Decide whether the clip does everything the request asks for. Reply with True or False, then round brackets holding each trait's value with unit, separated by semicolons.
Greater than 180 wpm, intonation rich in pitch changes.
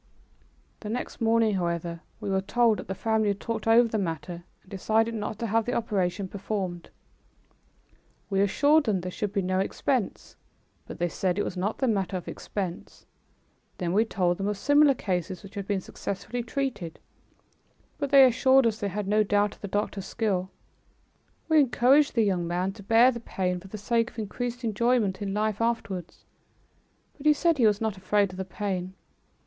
False (190 wpm; 3.5 semitones)